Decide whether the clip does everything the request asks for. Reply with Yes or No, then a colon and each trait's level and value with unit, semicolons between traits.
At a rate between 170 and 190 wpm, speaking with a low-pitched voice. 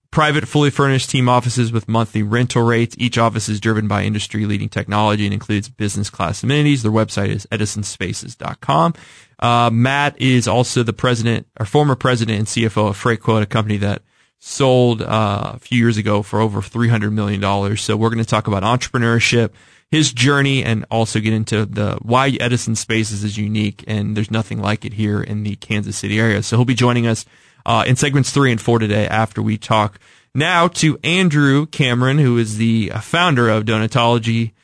Yes: average, 185 wpm; low, 115 Hz